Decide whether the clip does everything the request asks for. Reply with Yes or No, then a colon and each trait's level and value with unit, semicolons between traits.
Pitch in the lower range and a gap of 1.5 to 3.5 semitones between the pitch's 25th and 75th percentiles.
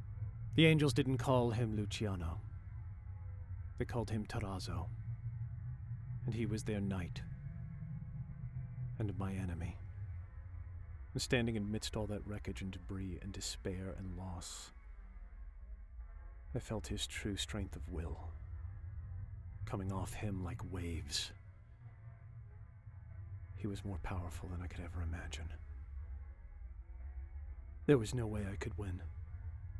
No: very low, 95 Hz; average, 4.2 semitones